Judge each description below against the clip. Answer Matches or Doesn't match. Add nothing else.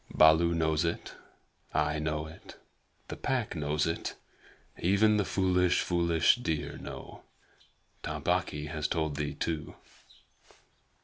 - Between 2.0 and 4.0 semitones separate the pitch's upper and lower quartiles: Matches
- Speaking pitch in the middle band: Doesn't match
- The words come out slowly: Matches